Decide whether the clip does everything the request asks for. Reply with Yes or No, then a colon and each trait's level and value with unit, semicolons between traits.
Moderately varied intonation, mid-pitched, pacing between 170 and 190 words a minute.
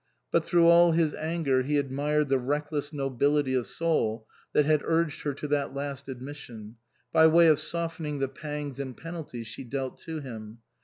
Yes: average, 3.0 semitones; medium, 145 Hz; average, 175 wpm